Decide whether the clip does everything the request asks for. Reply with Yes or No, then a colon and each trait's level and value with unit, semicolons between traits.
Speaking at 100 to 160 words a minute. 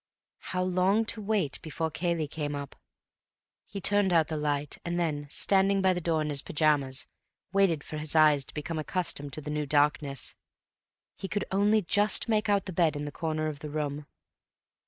No: average, 190 wpm